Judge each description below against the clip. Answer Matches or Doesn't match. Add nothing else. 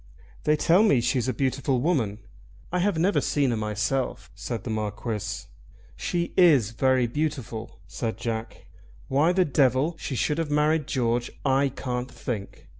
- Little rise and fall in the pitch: Doesn't match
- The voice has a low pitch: Matches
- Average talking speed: Matches